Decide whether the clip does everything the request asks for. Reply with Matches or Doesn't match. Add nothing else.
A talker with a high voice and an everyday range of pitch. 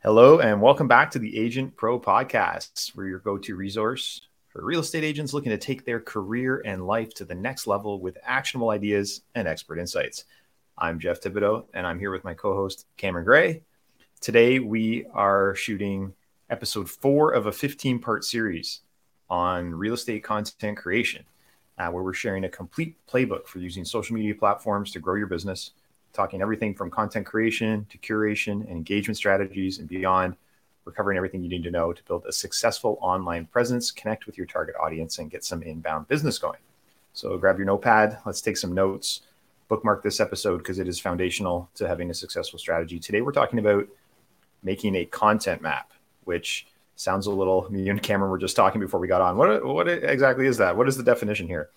Doesn't match